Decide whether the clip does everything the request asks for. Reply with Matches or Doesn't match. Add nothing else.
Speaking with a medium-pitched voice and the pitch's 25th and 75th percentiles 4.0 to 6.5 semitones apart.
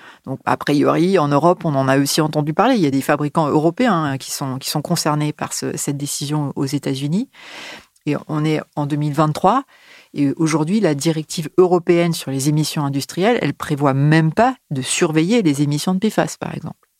Doesn't match